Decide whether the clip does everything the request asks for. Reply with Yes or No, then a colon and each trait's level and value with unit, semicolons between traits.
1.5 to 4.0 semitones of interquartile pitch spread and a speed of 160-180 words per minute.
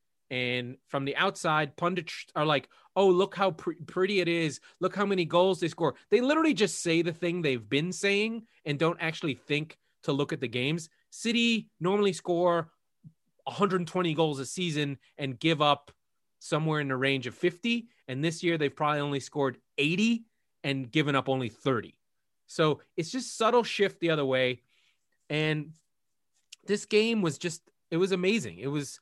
No: average, 5.0 semitones; average, 175 wpm